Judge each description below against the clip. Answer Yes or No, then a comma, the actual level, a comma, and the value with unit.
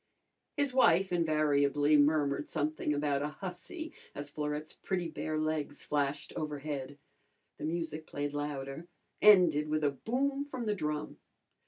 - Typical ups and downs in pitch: Yes, average, 3.1 semitones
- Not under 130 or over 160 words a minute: Yes, slow, 135 wpm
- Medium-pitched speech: Yes, medium, 150 Hz